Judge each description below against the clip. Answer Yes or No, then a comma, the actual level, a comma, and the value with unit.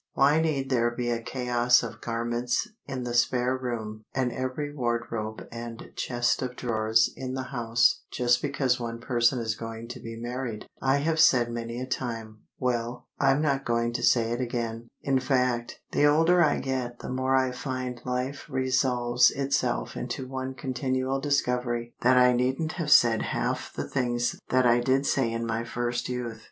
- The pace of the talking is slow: No, average, 175 wpm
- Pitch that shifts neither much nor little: No, narrow, 1.9 semitones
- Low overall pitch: Yes, low, 125 Hz